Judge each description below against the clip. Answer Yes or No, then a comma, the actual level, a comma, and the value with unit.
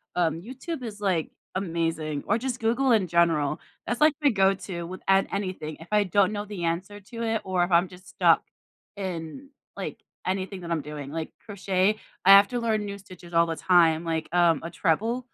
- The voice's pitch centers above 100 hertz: Yes, medium, 185 Hz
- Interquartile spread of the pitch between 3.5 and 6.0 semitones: Yes, average, 3.8 semitones